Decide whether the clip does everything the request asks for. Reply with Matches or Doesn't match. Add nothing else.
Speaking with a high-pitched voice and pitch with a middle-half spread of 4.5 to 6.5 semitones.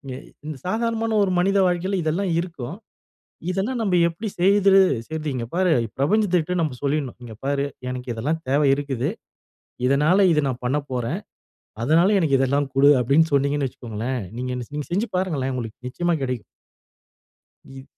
Doesn't match